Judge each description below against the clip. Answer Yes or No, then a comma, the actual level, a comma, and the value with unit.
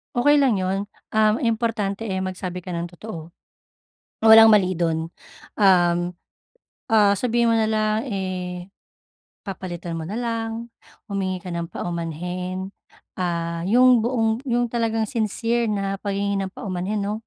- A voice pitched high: Yes, high, 200 Hz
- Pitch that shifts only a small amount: No, average, 3.7 semitones